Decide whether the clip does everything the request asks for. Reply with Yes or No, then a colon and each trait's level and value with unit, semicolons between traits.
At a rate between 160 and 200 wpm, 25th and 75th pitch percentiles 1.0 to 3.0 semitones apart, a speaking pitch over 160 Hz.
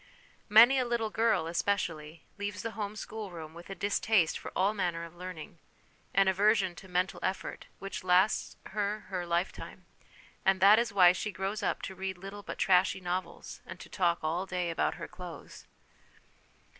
Yes: average, 175 wpm; average, 2.7 semitones; high, 190 Hz